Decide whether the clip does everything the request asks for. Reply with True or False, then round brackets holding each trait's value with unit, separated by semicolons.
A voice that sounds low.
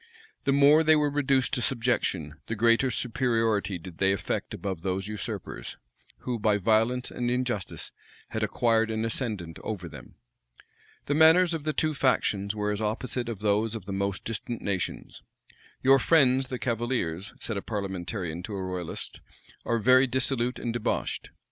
True (115 Hz)